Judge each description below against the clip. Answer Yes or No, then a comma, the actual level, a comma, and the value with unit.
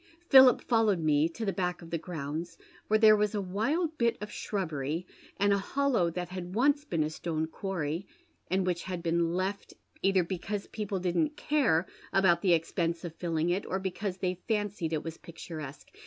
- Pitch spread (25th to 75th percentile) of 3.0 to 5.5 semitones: Yes, average, 3.7 semitones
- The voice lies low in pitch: No, medium, 185 Hz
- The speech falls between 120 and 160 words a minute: No, average, 185 wpm